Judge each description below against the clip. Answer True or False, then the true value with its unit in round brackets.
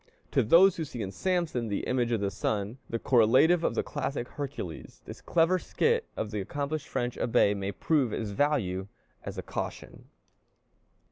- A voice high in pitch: False (125 Hz)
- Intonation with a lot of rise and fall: True (6.9 semitones)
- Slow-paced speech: False (175 wpm)